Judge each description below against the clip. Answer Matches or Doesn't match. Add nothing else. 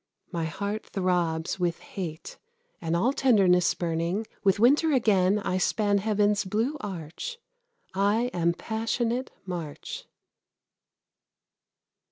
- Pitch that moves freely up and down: Doesn't match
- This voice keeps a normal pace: Doesn't match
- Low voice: Doesn't match